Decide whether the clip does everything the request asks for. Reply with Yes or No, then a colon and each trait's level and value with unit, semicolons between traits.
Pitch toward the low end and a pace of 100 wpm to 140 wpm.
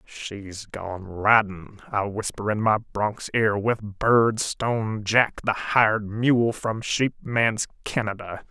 Yes: low, 110 Hz; slow, 135 wpm